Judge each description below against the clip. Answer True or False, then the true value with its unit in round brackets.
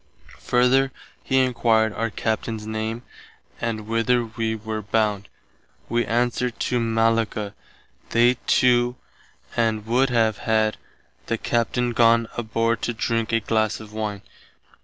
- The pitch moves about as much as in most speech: False (1.4 semitones)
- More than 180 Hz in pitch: False (115 Hz)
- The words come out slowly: True (125 wpm)